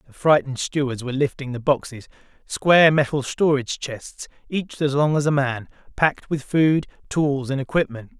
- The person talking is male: Yes, male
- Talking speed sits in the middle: Yes, average, 170 wpm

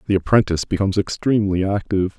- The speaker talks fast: No, slow, 135 wpm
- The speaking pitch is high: No, low, 100 Hz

